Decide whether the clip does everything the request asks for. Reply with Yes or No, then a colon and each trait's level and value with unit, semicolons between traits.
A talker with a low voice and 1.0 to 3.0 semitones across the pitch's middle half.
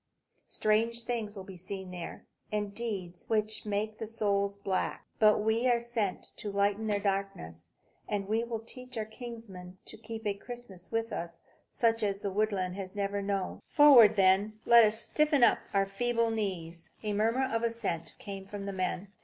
No: high, 210 Hz; narrow, 2.6 semitones